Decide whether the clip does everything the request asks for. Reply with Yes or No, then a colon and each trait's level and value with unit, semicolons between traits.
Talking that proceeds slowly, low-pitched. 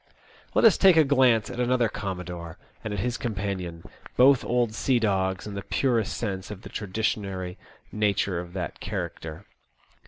No: average, 160 wpm; low, 105 Hz